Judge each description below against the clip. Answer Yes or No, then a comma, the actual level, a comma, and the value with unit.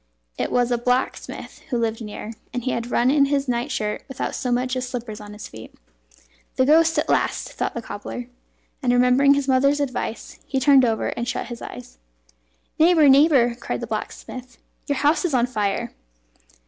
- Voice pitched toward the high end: Yes, very high, 250 Hz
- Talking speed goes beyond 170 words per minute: Yes, average, 190 wpm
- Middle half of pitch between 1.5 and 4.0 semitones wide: Yes, average, 2.9 semitones